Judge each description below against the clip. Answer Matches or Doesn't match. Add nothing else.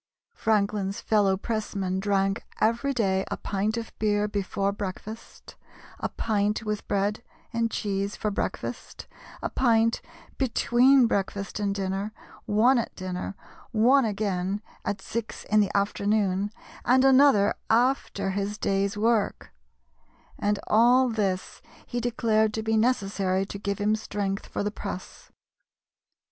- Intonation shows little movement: Matches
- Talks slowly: Matches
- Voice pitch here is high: Matches